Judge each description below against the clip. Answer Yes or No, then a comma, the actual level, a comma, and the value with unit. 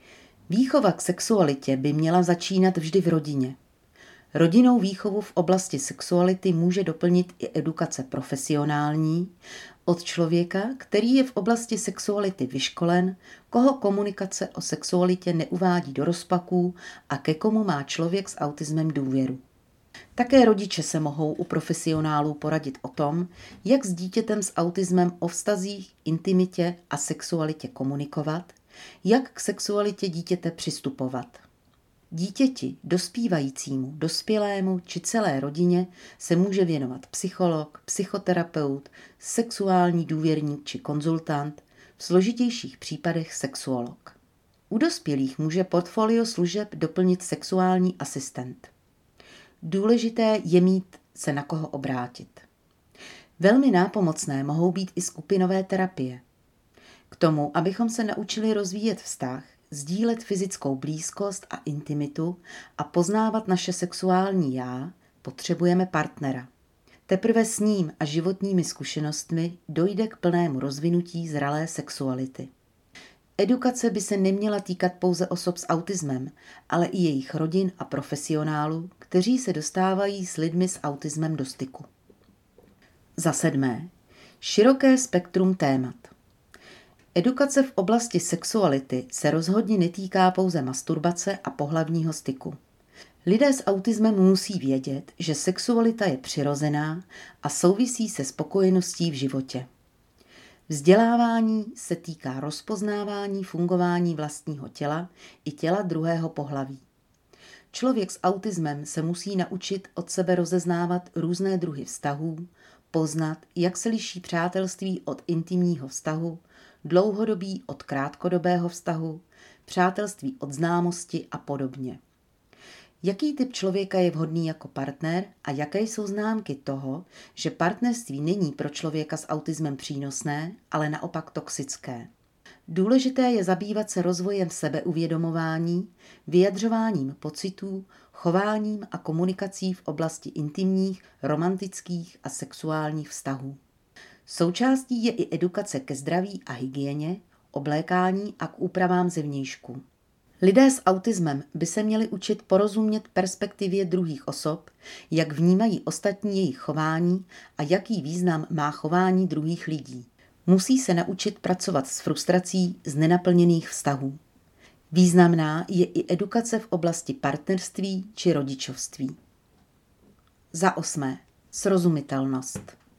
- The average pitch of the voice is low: No, medium, 175 Hz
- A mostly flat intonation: No, average, 4.1 semitones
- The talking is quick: No, slow, 115 wpm